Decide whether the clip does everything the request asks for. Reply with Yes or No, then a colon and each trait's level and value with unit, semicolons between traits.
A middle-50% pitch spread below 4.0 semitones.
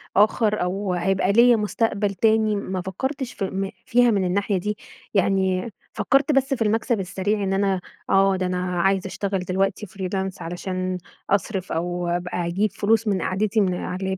Yes: narrow, 2.4 semitones